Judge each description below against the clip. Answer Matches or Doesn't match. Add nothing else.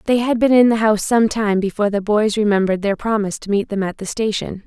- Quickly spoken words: Matches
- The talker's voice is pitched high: Matches